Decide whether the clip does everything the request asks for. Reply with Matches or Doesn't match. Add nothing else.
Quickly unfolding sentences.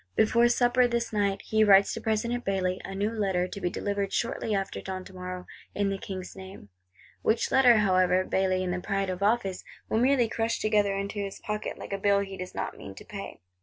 Matches